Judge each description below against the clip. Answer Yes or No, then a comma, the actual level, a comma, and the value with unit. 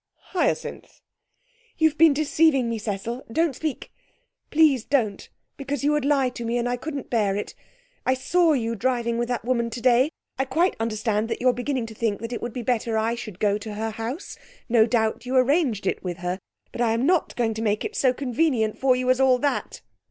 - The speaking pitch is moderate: No, high, 245 Hz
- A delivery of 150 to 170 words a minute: No, fast, 205 wpm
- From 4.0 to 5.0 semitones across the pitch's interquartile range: No, average, 3.6 semitones